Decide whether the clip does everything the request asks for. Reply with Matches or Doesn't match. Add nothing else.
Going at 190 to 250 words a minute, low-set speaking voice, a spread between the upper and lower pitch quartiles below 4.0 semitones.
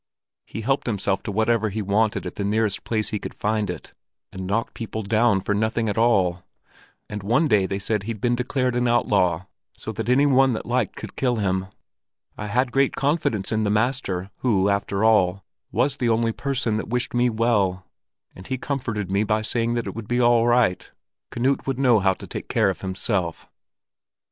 Matches